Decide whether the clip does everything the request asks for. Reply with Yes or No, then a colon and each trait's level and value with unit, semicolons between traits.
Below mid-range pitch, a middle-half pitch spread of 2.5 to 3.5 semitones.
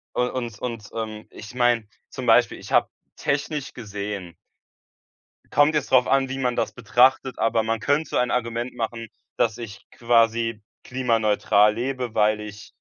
Yes: low, 115 Hz; average, 2.8 semitones